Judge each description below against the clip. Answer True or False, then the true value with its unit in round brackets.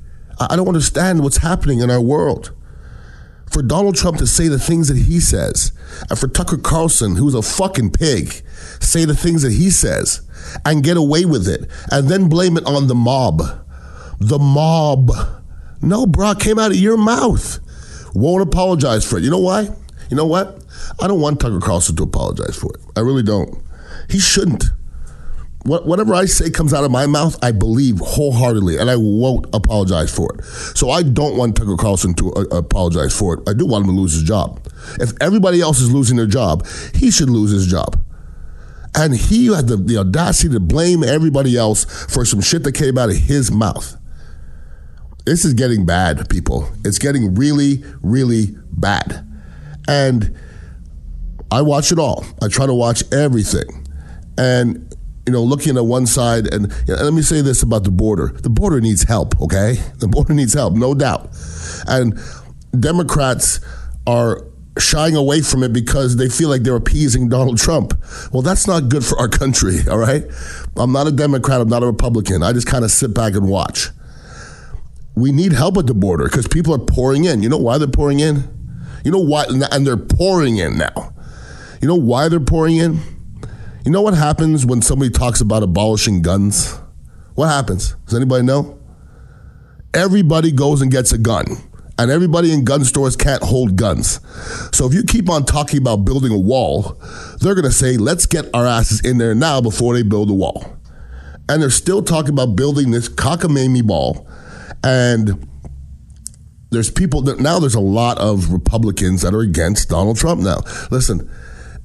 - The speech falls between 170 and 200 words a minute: True (185 wpm)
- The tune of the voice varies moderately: False (7.9 semitones)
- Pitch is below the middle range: True (120 Hz)